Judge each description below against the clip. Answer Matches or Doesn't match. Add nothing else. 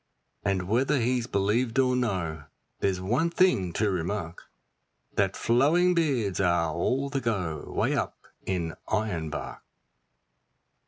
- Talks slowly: Matches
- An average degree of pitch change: Doesn't match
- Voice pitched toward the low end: Matches